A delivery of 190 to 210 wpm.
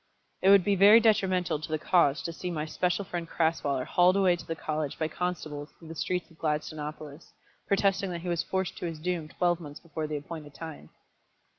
Yes: fast, 205 wpm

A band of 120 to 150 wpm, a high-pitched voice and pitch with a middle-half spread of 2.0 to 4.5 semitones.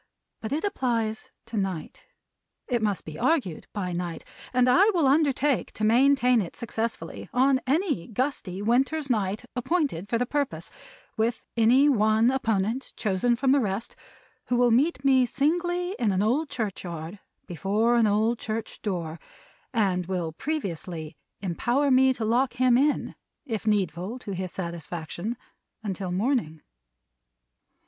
No: average, 140 wpm; high, 230 Hz; wide, 5.5 semitones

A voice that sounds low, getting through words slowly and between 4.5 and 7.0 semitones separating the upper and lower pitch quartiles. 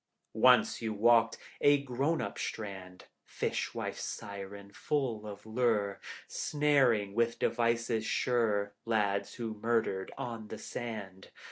No: low, 110 Hz; slow, 120 wpm; average, 2.8 semitones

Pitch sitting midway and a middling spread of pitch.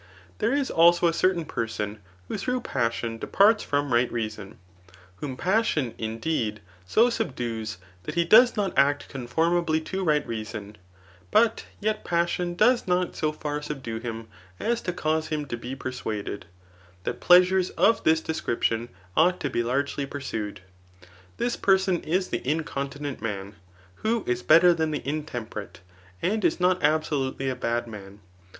No: medium, 150 Hz; wide, 7.2 semitones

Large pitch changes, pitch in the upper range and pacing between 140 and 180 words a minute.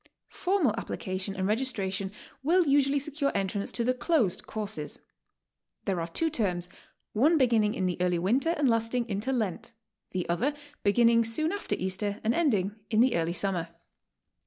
Yes: wide, 5.9 semitones; high, 220 Hz; average, 160 wpm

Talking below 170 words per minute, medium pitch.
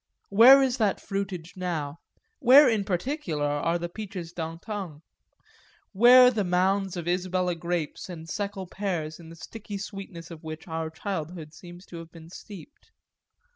Yes: average, 150 wpm; medium, 180 Hz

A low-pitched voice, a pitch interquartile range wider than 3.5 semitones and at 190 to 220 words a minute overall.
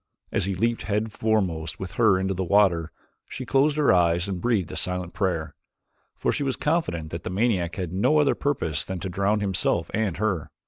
Yes: very low, 95 Hz; average, 4.1 semitones; average, 200 wpm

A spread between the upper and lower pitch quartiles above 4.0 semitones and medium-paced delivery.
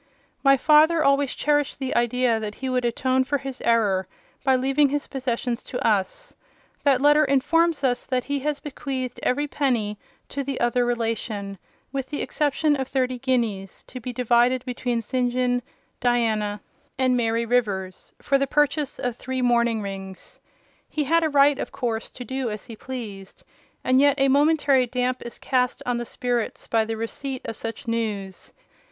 No: average, 3.0 semitones; average, 170 wpm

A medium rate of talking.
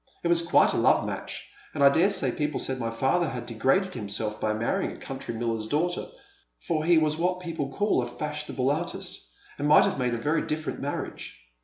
No: fast, 210 wpm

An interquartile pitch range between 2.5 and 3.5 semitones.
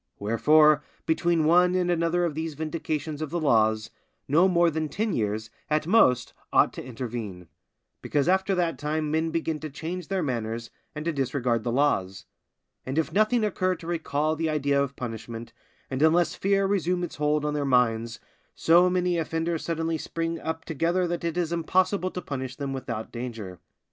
No: average, 4.8 semitones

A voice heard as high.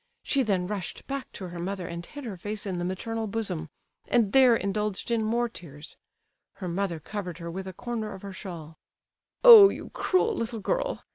Yes: high, 200 Hz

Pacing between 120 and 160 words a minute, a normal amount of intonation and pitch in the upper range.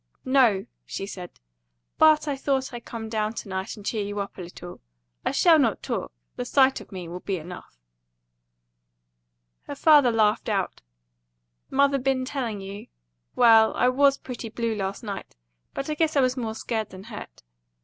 No: average, 175 wpm; average, 5.0 semitones; high, 225 Hz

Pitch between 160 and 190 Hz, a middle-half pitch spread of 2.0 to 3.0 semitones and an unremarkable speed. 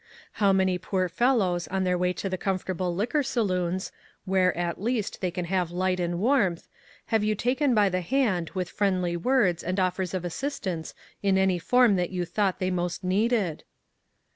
Yes: medium, 185 Hz; average, 2.7 semitones; average, 180 wpm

